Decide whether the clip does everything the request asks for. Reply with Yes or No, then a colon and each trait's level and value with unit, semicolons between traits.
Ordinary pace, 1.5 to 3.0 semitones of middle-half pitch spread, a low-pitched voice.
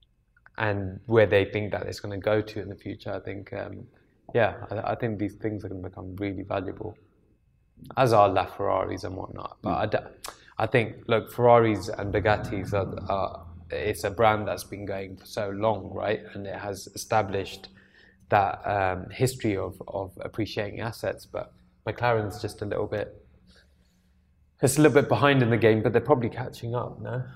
Yes: average, 180 wpm; narrow, 2.6 semitones; low, 105 Hz